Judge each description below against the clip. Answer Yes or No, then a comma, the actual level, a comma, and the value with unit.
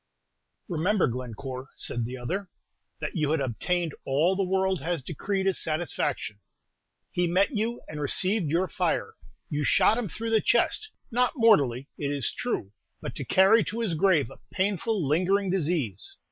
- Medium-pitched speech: Yes, medium, 175 Hz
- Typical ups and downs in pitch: No, wide, 5.8 semitones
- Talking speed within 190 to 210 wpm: No, average, 160 wpm